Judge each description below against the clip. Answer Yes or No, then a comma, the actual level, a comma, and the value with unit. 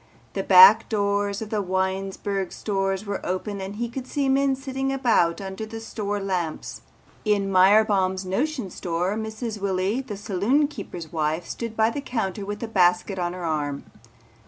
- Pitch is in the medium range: No, high, 200 Hz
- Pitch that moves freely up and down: No, average, 3.2 semitones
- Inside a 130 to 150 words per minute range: No, average, 165 wpm